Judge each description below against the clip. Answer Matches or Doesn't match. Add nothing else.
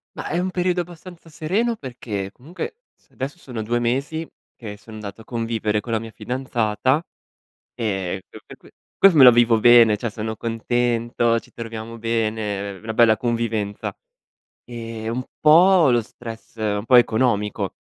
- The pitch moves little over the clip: Doesn't match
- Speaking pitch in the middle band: Doesn't match